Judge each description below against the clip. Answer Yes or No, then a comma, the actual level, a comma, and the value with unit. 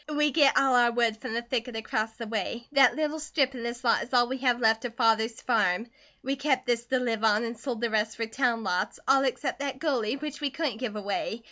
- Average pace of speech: No, fast, 245 wpm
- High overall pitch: Yes, high, 240 Hz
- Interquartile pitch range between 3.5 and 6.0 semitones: No, average, 3.1 semitones